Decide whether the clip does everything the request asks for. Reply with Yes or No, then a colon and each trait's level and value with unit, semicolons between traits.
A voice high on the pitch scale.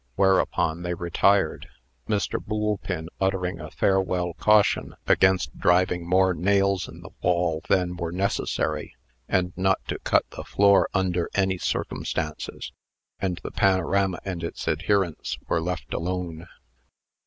No: very low, 90 Hz